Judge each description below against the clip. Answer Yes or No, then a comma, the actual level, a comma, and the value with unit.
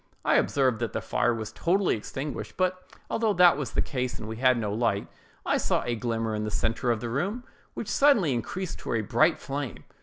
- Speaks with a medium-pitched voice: No, low, 130 Hz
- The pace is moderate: No, fast, 215 wpm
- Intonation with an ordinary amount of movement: No, wide, 7.4 semitones